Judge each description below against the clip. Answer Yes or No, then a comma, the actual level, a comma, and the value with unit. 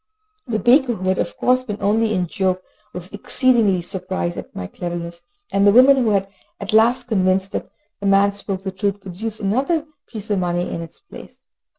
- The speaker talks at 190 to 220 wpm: Yes, average, 195 wpm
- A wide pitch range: No, average, 3.3 semitones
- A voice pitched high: Yes, high, 200 Hz